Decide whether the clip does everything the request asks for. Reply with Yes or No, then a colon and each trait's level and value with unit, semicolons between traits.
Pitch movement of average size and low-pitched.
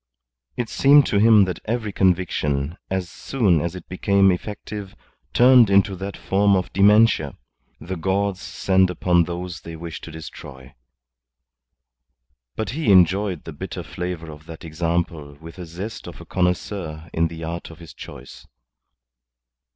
Yes: average, 3.4 semitones; very low, 90 Hz